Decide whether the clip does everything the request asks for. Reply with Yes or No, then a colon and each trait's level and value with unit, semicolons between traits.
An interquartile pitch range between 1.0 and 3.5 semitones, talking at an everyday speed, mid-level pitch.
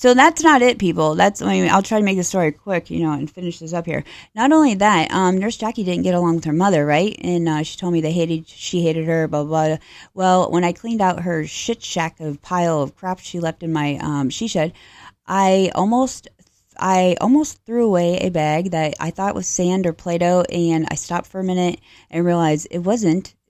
No: average, 3.1 semitones; fast, 240 wpm; medium, 175 Hz